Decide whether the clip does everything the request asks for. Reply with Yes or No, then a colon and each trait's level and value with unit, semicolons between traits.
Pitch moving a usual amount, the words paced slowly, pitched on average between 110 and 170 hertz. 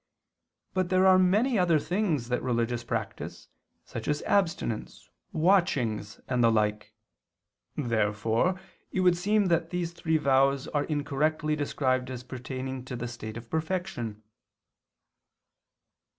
No: wide, 6.8 semitones; slow, 125 wpm; medium, 140 Hz